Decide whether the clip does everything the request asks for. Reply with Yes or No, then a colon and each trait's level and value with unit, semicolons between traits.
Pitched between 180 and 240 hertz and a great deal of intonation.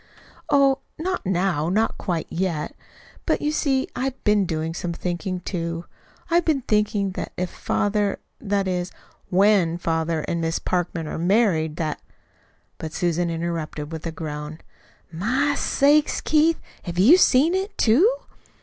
Yes: medium, 185 Hz; wide, 7.3 semitones